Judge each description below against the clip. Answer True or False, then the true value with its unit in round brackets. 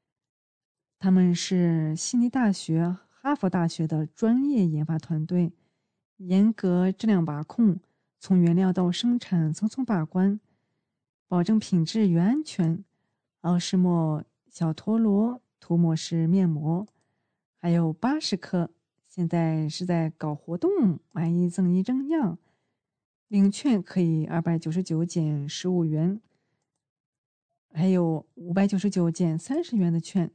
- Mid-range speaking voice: True (175 Hz)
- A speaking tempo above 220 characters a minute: False (190 characters per minute)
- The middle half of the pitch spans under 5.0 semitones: True (3.5 semitones)